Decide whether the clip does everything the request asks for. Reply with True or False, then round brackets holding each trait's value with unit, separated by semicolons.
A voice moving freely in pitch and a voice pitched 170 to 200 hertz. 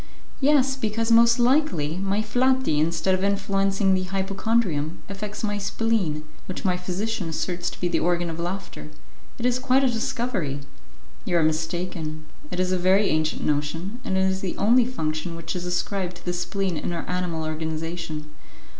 False (4.7 semitones; 185 Hz)